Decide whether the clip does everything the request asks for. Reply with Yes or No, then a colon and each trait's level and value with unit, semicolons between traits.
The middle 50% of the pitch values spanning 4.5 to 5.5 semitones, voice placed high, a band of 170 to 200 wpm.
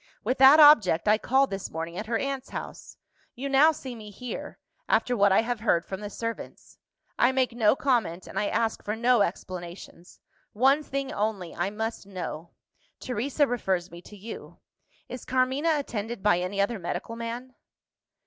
Yes: average, 4.8 semitones; high, 225 Hz; average, 175 wpm